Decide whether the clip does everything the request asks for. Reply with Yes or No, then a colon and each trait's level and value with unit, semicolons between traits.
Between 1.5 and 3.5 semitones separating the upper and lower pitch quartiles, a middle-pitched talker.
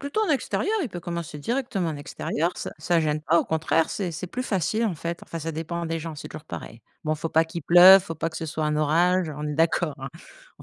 Yes: average, 2.8 semitones; medium, 165 Hz